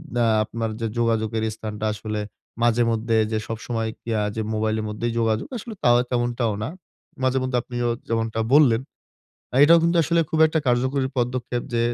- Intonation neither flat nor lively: No, narrow, 2.0 semitones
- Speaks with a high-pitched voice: No, low, 120 Hz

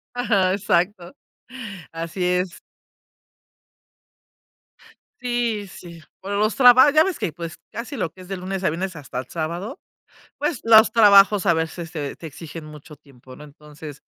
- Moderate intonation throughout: Yes, average, 4.5 semitones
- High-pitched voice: No, medium, 180 Hz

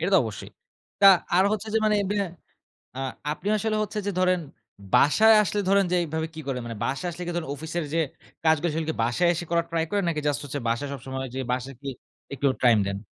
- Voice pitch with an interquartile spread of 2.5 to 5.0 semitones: No, wide, 5.5 semitones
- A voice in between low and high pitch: Yes, medium, 165 Hz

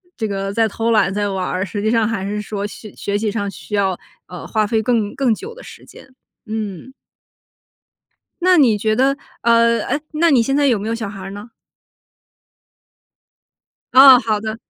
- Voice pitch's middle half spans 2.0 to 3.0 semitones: Yes, narrow, 2.6 semitones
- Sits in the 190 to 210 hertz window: No, high, 220 Hz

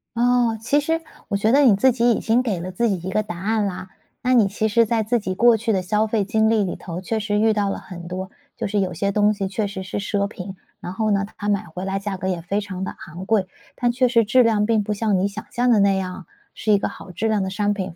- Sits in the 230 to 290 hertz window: No, high, 205 Hz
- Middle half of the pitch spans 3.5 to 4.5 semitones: No, average, 2.8 semitones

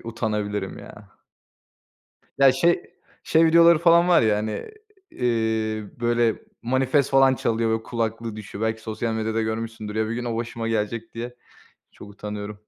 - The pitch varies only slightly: Yes, narrow, 2.1 semitones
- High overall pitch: No, low, 115 Hz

